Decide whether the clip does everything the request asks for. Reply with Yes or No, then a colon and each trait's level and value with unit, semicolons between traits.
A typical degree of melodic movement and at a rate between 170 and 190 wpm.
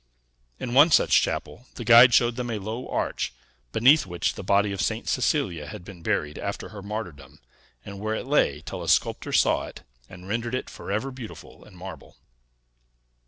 Yes: average, 4.0 semitones; average, 180 wpm